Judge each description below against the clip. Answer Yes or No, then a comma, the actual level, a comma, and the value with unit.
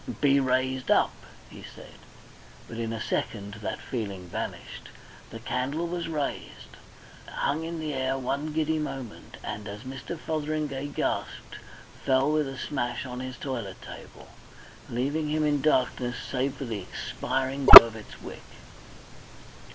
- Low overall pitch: Yes, low, 130 Hz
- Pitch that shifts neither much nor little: Yes, average, 3.6 semitones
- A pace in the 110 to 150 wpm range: Yes, average, 145 wpm